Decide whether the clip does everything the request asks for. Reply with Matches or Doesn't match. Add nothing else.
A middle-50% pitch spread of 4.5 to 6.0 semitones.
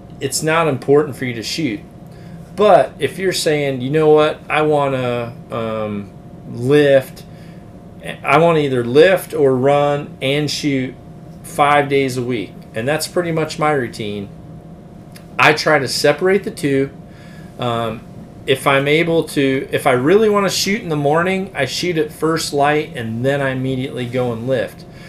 Doesn't match